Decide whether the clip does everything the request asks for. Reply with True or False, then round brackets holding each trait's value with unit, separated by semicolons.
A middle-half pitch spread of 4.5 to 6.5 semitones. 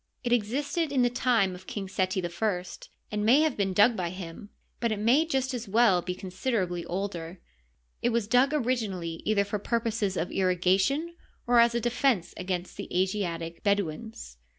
True (4.8 semitones)